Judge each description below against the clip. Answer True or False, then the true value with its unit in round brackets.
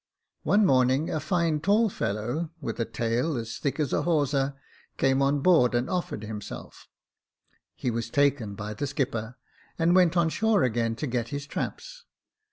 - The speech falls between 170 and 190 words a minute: True (175 wpm)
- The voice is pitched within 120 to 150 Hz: True (140 Hz)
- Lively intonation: True (5.8 semitones)